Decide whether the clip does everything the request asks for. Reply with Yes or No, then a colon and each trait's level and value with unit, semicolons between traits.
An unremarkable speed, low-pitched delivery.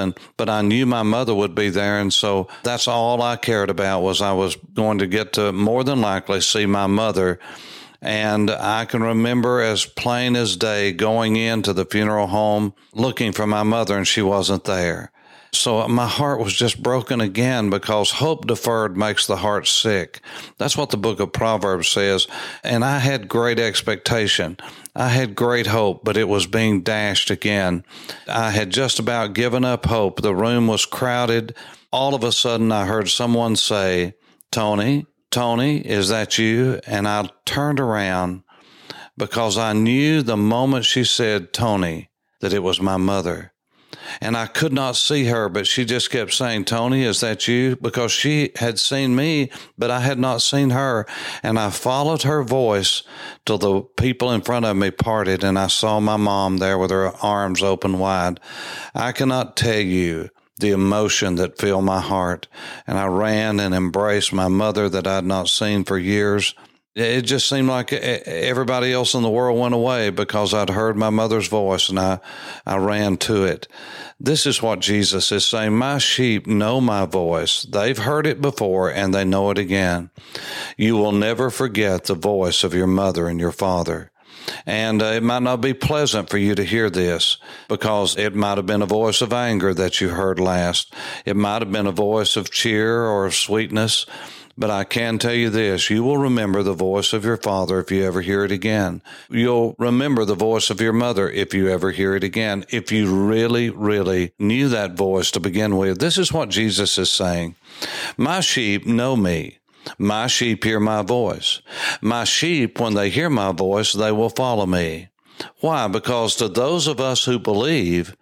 Yes: average, 185 wpm; low, 110 Hz